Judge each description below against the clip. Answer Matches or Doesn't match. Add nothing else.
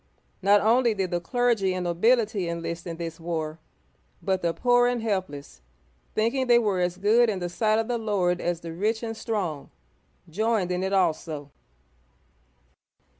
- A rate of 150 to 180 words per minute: Matches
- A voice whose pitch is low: Doesn't match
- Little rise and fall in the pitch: Doesn't match